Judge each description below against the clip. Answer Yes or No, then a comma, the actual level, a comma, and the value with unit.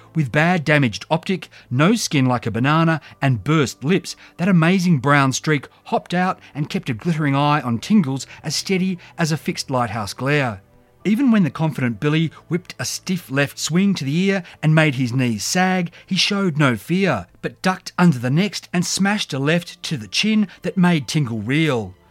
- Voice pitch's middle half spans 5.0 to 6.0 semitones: Yes, wide, 5.6 semitones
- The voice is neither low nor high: Yes, medium, 155 Hz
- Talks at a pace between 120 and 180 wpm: No, average, 190 wpm